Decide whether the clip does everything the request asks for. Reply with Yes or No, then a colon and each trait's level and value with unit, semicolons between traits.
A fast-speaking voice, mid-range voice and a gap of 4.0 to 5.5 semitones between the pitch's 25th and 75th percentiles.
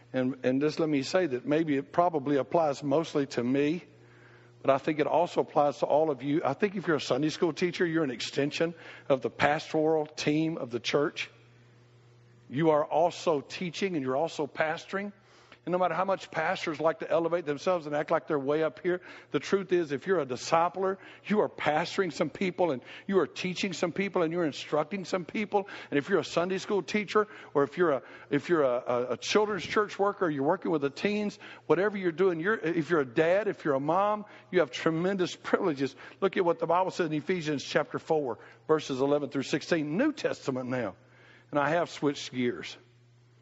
Yes: fast, 210 wpm; medium, 155 Hz; average, 4.5 semitones